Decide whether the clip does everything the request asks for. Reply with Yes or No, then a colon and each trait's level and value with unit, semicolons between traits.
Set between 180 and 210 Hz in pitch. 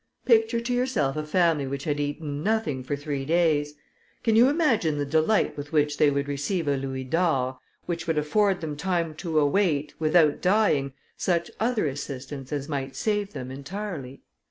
No: medium, 155 Hz